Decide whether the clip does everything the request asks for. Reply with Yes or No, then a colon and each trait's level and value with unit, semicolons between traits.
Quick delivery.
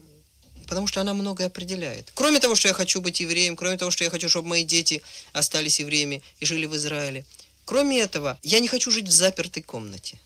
Yes: fast, 205 wpm